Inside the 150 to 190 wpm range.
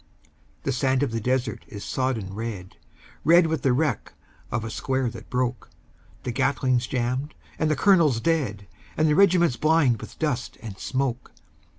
Yes: average, 165 wpm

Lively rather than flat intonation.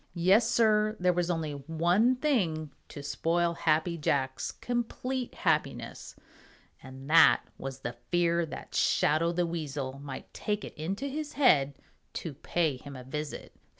Yes: wide, 5.9 semitones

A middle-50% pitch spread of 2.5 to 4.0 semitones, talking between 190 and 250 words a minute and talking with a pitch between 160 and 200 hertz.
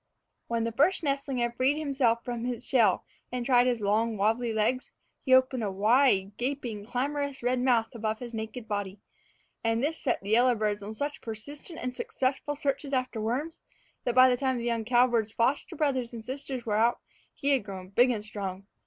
No: average, 3.1 semitones; average, 195 wpm; high, 240 Hz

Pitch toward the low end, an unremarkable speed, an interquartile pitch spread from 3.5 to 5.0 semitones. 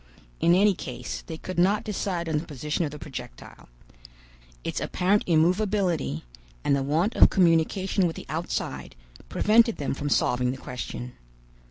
No: medium, 165 Hz; average, 155 wpm; average, 4.7 semitones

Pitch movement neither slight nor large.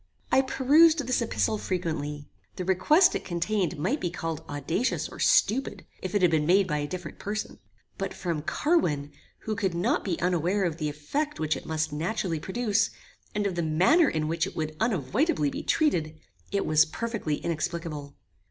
No: wide, 5.9 semitones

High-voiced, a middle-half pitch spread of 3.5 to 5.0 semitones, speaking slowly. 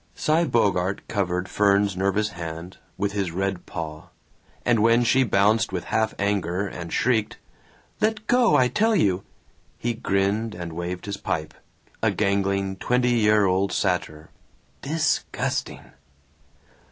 No: low, 100 Hz; average, 4.0 semitones; slow, 130 wpm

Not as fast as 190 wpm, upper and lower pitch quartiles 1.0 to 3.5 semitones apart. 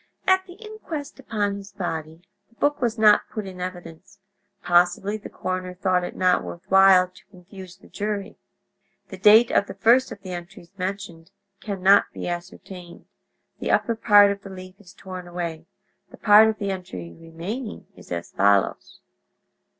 Yes: average, 170 wpm; average, 2.8 semitones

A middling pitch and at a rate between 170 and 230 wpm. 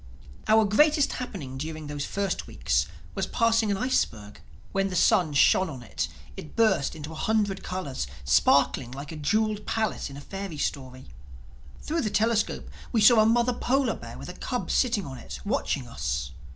No: high, 195 Hz; average, 180 wpm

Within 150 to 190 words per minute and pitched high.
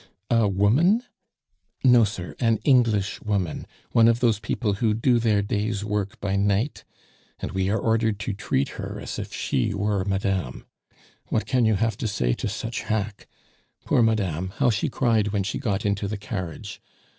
No: average, 175 wpm; low, 105 Hz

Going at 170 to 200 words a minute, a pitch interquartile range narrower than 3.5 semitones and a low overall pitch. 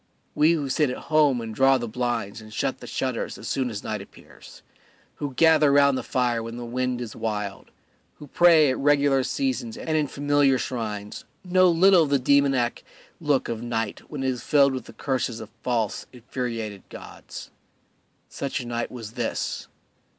No: average, 180 wpm; average, 3.8 semitones; low, 130 Hz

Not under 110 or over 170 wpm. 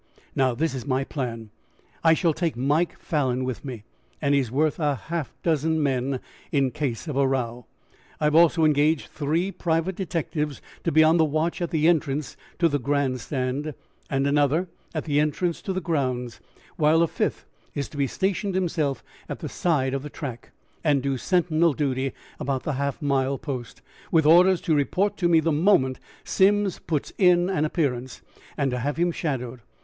No: average, 185 wpm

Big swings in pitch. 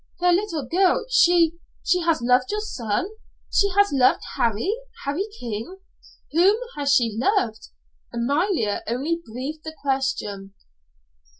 Yes: wide, 7.0 semitones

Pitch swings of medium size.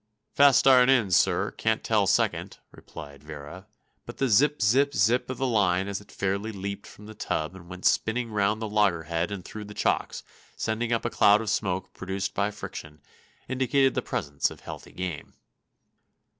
Yes: average, 3.7 semitones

